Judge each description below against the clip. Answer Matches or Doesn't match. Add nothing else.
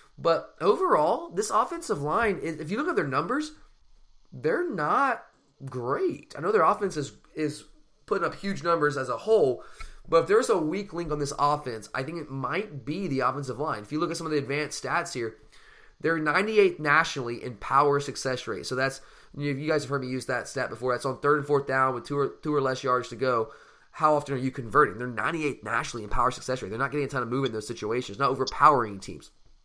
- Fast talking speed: Matches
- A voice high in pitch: Doesn't match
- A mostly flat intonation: Doesn't match